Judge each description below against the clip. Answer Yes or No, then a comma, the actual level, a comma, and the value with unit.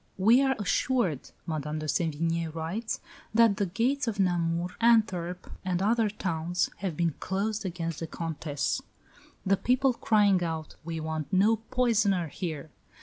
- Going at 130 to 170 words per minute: Yes, average, 145 wpm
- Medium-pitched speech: Yes, medium, 180 Hz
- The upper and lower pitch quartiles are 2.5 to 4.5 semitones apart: No, average, 4.9 semitones